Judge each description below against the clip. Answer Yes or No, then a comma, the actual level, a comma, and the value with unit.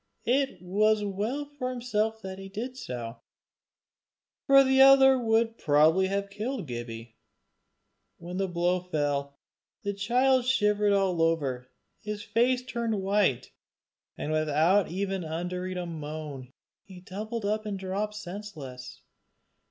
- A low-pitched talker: No, high, 195 Hz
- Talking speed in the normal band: No, slow, 130 wpm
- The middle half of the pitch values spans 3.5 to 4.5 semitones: No, wide, 5.4 semitones